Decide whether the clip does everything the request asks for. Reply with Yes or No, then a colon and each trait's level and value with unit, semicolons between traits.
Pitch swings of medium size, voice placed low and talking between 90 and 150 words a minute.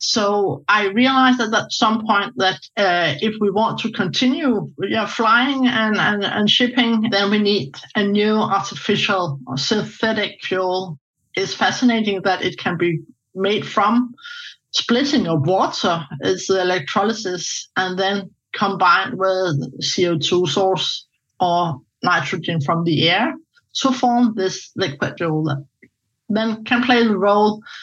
No: average, 3.9 semitones; high, 200 Hz; average, 140 wpm